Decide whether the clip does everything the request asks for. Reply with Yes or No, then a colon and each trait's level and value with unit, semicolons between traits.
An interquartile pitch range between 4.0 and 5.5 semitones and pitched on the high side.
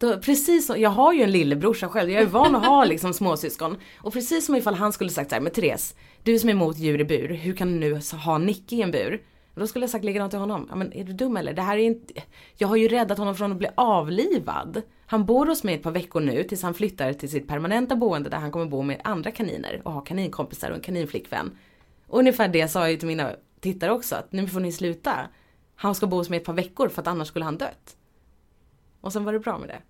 Yes: average, 5.2 semitones; high, 195 Hz